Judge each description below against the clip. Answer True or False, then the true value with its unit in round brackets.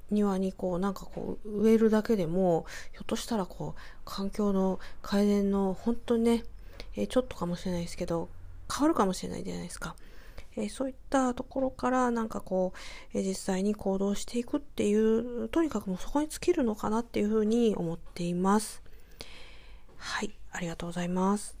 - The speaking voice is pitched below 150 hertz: False (205 Hz)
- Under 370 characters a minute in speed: False (390 characters per minute)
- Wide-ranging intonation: False (3.9 semitones)